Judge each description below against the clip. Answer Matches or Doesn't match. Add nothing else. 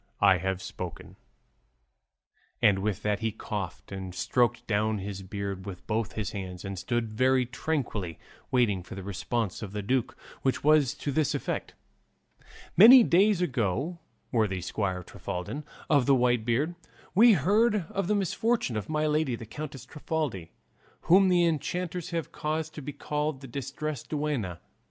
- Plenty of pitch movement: Matches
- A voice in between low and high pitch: Doesn't match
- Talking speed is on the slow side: Doesn't match